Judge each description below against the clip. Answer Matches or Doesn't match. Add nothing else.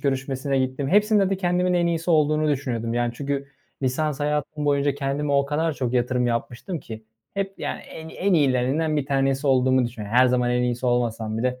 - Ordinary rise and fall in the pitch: Matches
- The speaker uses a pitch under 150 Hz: Matches